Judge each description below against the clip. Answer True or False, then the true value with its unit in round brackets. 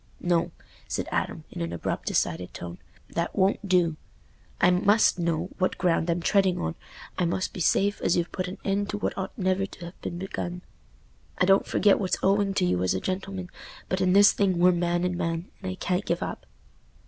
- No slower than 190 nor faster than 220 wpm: True (205 wpm)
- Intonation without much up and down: True (2.2 semitones)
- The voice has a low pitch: False (180 Hz)